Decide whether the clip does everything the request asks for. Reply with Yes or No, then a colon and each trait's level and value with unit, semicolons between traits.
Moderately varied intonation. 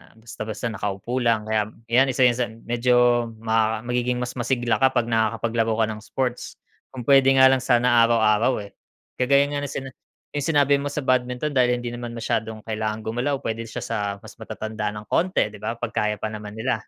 No: narrow, 2.2 semitones